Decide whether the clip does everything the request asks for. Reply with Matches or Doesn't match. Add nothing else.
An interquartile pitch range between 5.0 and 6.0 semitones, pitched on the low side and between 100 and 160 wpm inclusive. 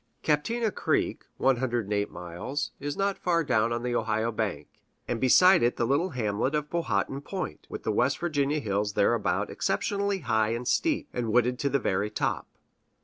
Doesn't match